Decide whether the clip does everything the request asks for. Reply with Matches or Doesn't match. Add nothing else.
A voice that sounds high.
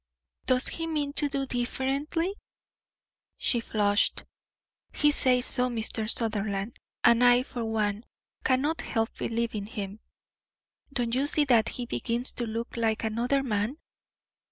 Matches